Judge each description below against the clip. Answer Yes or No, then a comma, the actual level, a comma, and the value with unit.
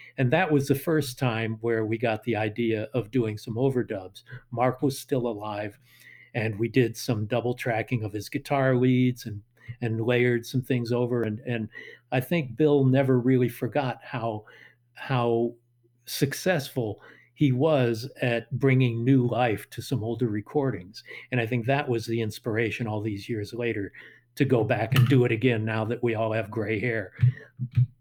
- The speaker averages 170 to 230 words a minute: Yes, average, 175 wpm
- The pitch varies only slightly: Yes, narrow, 2.3 semitones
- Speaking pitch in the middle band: No, low, 120 Hz